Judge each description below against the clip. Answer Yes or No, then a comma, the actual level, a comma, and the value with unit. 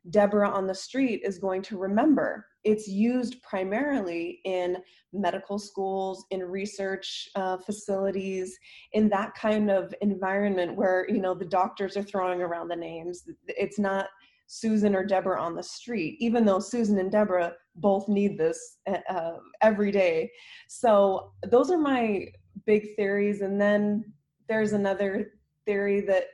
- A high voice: Yes, high, 200 Hz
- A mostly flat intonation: Yes, narrow, 2.0 semitones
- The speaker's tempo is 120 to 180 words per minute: Yes, average, 145 wpm